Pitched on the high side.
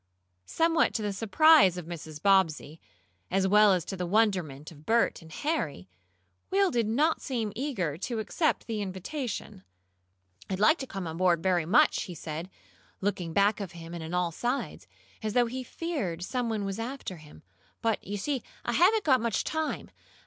Yes: high, 205 Hz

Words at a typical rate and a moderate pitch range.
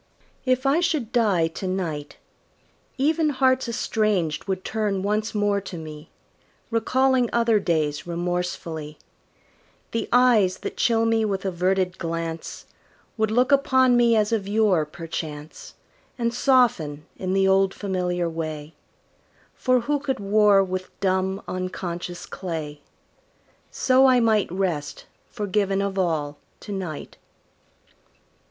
No: slow, 125 wpm; average, 5.0 semitones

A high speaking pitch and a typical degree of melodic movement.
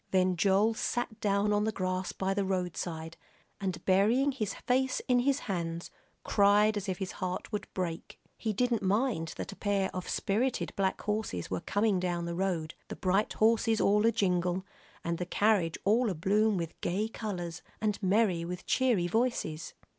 Yes: high, 195 Hz; average, 3.4 semitones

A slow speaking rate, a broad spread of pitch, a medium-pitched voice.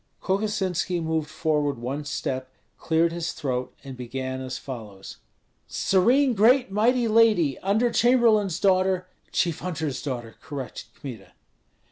Yes: slow, 125 wpm; wide, 7.6 semitones; medium, 160 Hz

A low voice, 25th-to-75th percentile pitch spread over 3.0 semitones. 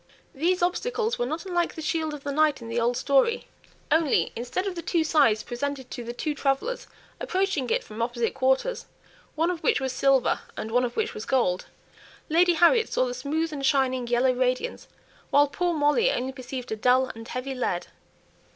No: very high, 280 Hz; wide, 5.5 semitones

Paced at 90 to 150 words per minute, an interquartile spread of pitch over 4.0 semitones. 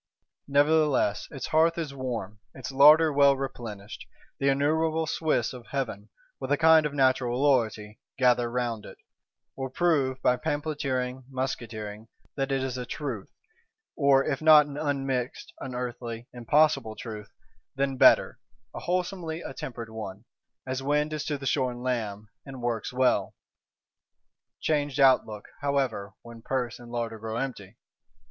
No: average, 140 wpm; average, 3.4 semitones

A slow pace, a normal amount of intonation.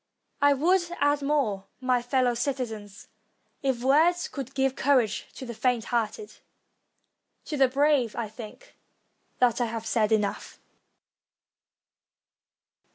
Yes: slow, 125 wpm; average, 3.8 semitones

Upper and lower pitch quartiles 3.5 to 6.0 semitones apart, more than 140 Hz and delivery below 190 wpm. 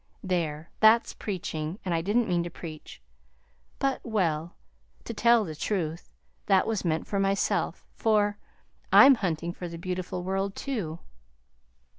Yes: average, 4.0 semitones; medium, 185 Hz; average, 140 wpm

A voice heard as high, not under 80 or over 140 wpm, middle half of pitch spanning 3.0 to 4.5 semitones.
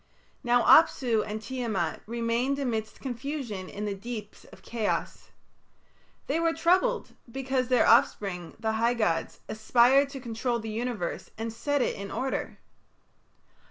Yes: high, 235 Hz; slow, 135 wpm; average, 3.4 semitones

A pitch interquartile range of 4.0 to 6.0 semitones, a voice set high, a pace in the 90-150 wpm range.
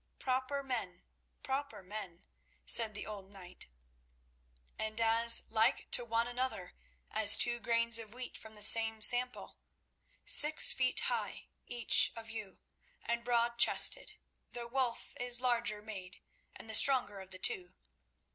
No: narrow, 2.4 semitones; high, 230 Hz; average, 140 wpm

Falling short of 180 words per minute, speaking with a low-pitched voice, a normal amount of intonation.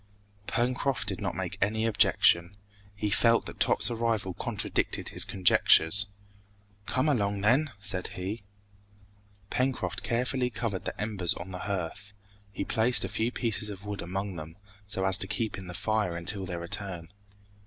Yes: average, 155 wpm; low, 100 Hz; average, 3.4 semitones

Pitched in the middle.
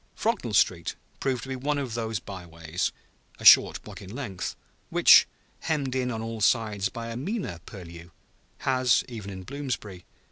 No: low, 115 Hz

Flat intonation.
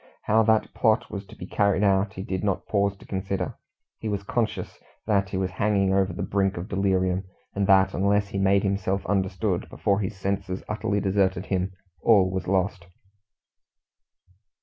Yes: narrow, 1.3 semitones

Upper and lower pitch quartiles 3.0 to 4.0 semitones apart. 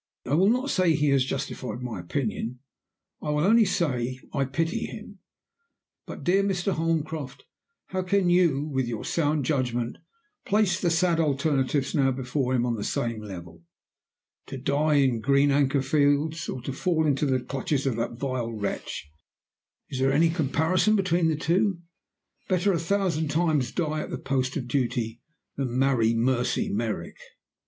No: average, 4.6 semitones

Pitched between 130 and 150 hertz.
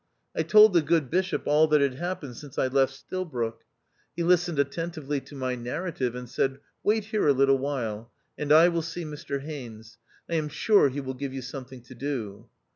Yes: medium, 140 Hz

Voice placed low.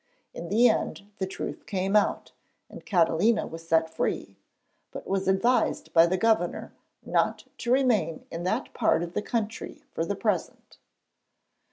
No: high, 190 Hz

